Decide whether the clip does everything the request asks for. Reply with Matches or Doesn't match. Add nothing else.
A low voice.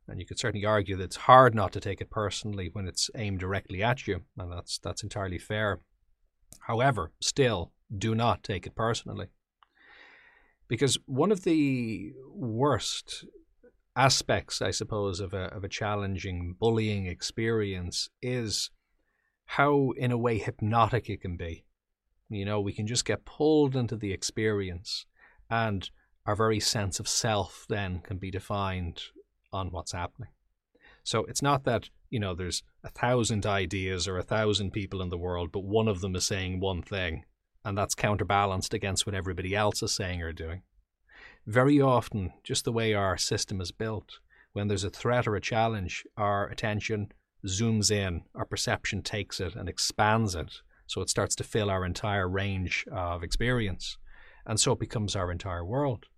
Matches